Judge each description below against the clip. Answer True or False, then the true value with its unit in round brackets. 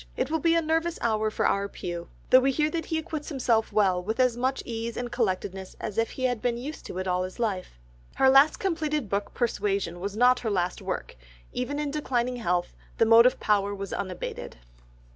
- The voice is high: True (235 Hz)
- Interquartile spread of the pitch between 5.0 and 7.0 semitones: True (5.4 semitones)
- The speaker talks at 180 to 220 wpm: True (205 wpm)